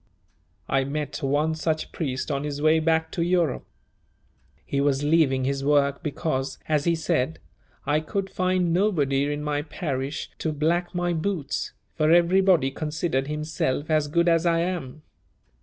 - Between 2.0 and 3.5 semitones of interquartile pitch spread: Yes, average, 3.0 semitones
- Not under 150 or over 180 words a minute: Yes, average, 155 wpm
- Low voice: No, medium, 155 Hz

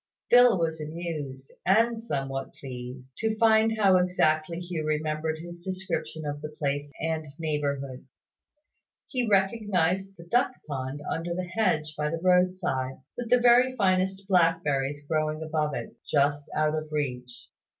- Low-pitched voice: No, medium, 160 Hz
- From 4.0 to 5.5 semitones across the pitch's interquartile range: Yes, average, 4.4 semitones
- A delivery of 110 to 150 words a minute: Yes, average, 145 wpm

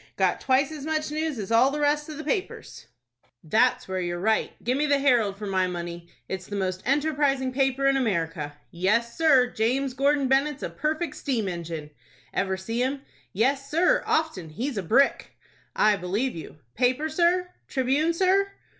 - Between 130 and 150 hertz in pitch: No, very high, 260 Hz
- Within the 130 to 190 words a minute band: Yes, average, 175 wpm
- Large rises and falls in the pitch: Yes, wide, 7.1 semitones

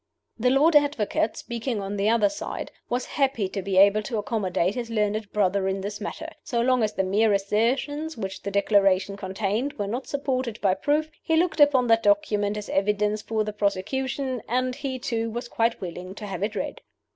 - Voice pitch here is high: Yes, high, 215 Hz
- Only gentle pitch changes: No, average, 4.1 semitones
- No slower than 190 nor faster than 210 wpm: Yes, average, 195 wpm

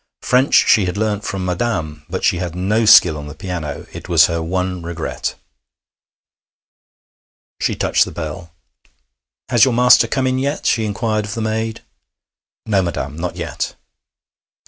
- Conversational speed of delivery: Yes, average, 155 wpm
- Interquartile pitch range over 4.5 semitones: Yes, average, 4.9 semitones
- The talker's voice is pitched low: Yes, very low, 95 Hz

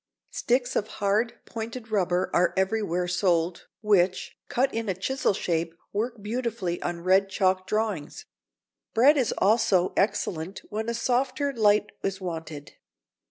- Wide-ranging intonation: No, average, 4.2 semitones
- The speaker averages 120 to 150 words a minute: Yes, slow, 135 wpm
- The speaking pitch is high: Yes, high, 205 Hz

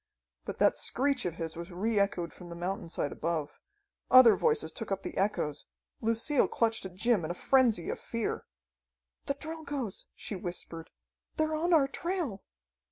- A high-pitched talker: Yes, high, 215 Hz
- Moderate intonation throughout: No, wide, 7.8 semitones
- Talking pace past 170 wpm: No, average, 165 wpm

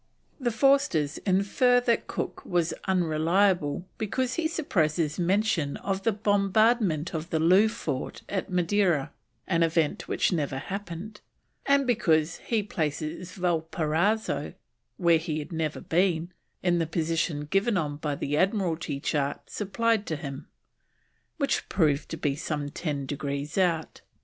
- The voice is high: No, medium, 170 Hz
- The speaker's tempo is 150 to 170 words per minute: No, slow, 135 wpm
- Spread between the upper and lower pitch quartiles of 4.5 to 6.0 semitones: Yes, average, 4.8 semitones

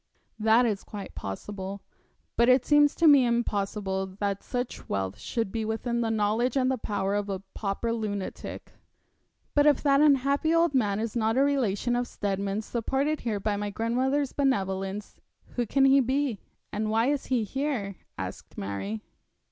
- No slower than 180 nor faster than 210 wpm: No, average, 165 wpm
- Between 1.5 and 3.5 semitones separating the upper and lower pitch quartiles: No, average, 4.8 semitones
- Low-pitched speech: No, high, 225 Hz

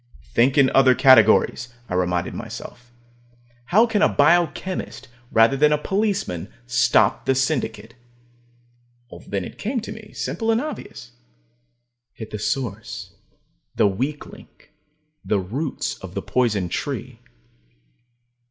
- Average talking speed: No, slow, 125 wpm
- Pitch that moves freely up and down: Yes, wide, 7.6 semitones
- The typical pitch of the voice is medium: No, low, 130 Hz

